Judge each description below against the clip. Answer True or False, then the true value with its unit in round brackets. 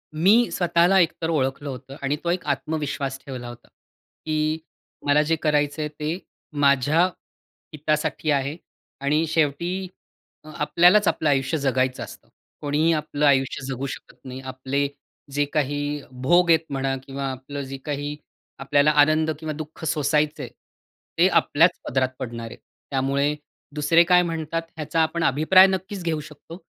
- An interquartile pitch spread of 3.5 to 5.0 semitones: False (2.9 semitones)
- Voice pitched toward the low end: False (150 Hz)